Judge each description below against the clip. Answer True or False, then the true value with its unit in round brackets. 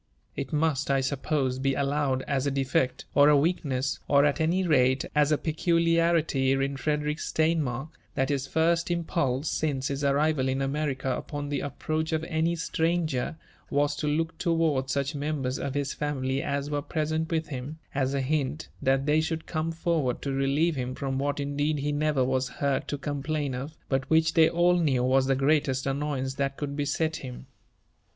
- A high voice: False (145 Hz)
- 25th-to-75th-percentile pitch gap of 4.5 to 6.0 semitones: False (2.7 semitones)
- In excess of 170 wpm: True (180 wpm)